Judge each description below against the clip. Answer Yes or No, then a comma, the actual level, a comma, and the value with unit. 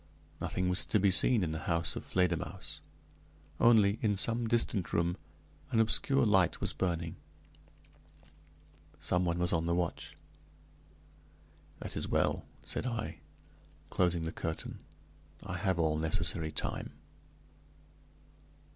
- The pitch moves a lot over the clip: No, average, 4.0 semitones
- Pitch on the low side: Yes, very low, 90 Hz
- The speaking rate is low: Yes, slow, 125 wpm